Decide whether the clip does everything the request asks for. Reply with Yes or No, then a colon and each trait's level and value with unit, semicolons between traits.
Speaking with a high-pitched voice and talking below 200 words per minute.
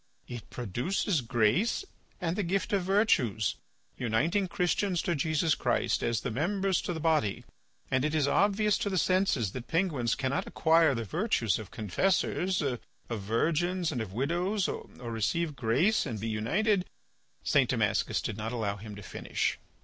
No: medium, 155 Hz; average, 165 wpm